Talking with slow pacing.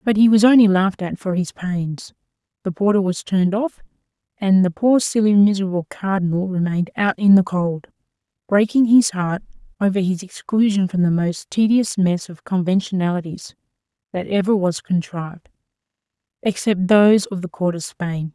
No: average, 155 wpm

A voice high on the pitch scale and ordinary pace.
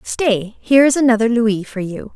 Yes: high, 230 Hz; average, 195 wpm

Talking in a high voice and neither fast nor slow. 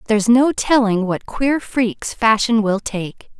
Yes: high, 225 Hz; average, 160 wpm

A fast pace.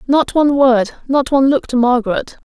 No: average, 195 wpm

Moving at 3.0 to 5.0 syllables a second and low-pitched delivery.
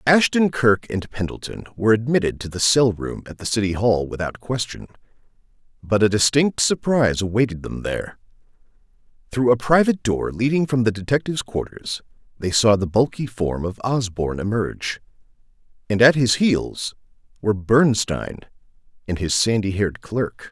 No: 5.3 syllables/s; low, 115 Hz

